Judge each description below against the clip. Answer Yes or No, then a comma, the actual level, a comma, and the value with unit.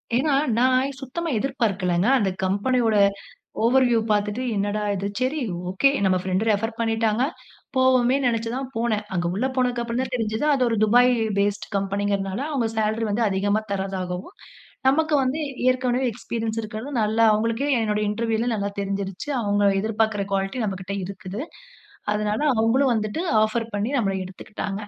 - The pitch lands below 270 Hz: Yes, high, 220 Hz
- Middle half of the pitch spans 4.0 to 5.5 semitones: No, average, 3.5 semitones